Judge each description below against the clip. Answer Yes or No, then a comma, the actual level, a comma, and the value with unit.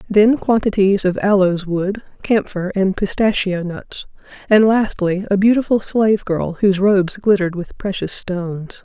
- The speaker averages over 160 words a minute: No, average, 145 wpm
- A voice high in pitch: Yes, high, 195 Hz